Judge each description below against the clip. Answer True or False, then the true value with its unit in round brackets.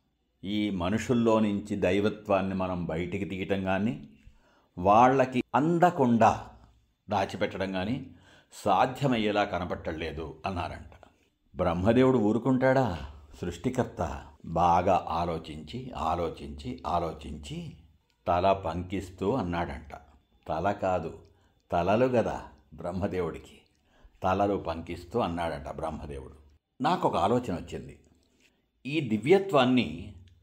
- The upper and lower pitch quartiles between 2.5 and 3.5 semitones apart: False (5.0 semitones)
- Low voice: True (95 Hz)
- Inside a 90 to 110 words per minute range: False (80 wpm)